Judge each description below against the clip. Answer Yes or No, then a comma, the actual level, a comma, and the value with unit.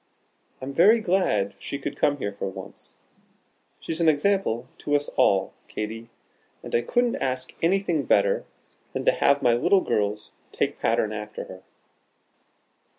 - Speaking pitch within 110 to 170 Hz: Yes, low, 135 Hz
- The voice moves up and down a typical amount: No, wide, 8.1 semitones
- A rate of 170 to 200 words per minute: No, average, 150 wpm